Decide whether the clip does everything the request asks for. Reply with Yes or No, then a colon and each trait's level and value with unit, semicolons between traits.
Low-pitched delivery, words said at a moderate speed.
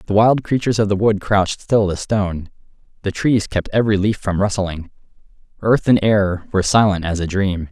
Yes: low, 100 Hz; average, 195 wpm